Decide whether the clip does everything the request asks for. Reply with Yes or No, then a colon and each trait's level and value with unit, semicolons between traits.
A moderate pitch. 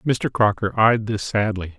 No: low, 110 Hz